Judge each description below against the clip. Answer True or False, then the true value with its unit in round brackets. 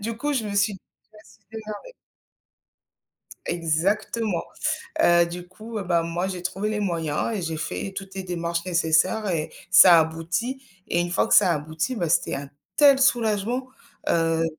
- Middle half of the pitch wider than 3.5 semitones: True (4.3 semitones)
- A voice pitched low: False (185 Hz)